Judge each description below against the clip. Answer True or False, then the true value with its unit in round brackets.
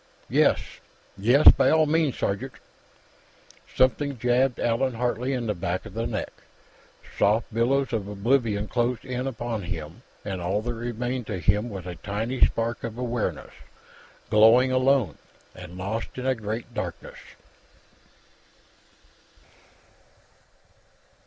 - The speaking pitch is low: True (115 Hz)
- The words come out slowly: True (125 wpm)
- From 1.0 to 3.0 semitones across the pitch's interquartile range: False (3.5 semitones)